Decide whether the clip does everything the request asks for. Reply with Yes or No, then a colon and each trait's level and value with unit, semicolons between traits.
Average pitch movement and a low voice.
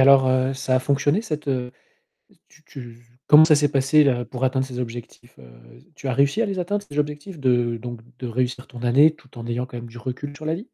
Yes: average, 3.3 semitones; low, 130 Hz